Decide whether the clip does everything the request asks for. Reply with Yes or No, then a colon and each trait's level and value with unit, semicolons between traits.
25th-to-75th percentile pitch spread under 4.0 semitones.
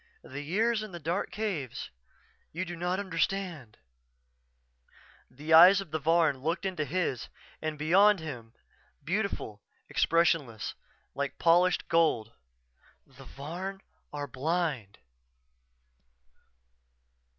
No: average, 4.5 semitones